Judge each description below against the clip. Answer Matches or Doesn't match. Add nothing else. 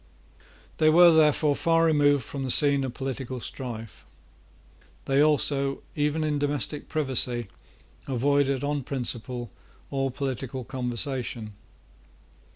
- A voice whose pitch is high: Doesn't match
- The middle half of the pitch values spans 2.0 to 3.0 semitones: Matches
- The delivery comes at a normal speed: Doesn't match